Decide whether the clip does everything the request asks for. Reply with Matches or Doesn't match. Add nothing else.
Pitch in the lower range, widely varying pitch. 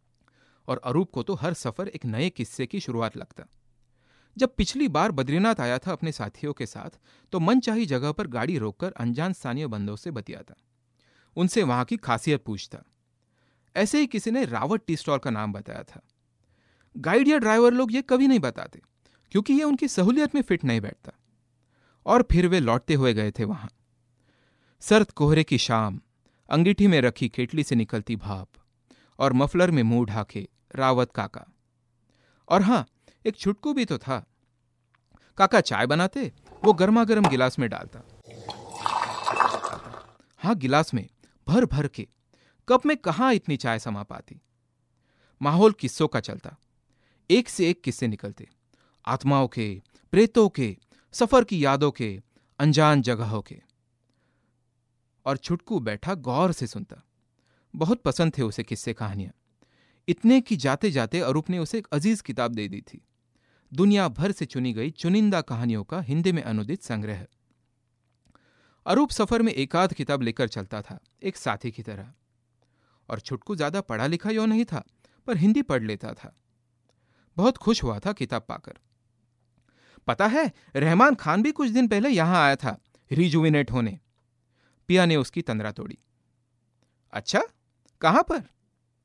Matches